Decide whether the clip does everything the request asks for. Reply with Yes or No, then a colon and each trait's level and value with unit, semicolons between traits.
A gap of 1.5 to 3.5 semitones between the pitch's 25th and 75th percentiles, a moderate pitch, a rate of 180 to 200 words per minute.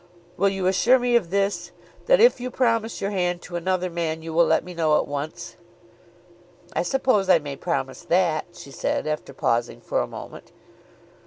No: average, 4.0 semitones; medium, 180 Hz; average, 185 wpm